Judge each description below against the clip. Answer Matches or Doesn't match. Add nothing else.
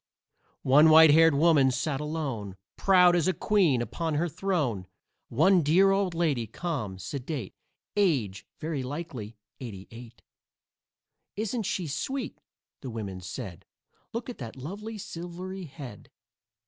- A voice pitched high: Doesn't match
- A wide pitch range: Matches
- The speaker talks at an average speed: Doesn't match